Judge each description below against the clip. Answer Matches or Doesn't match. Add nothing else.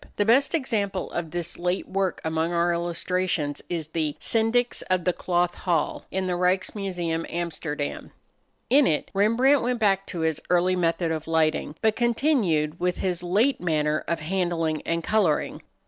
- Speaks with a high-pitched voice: Doesn't match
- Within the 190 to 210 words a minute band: Doesn't match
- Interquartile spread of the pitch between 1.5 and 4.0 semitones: Matches